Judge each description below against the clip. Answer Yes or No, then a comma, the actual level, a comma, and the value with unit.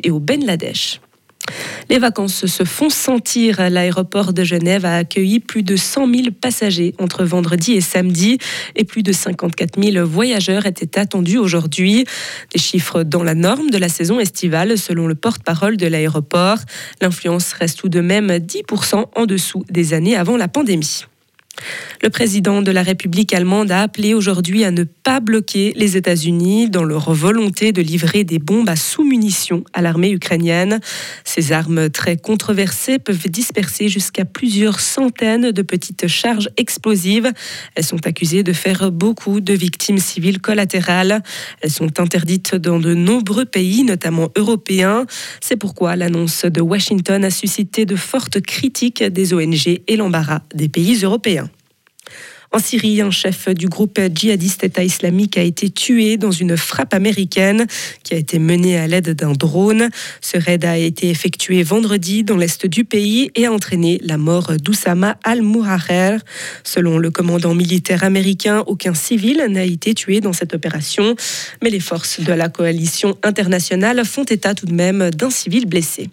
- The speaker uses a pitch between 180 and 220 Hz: Yes, high, 190 Hz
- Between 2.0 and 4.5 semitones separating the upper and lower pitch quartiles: Yes, average, 3.5 semitones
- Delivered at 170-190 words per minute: No, average, 160 wpm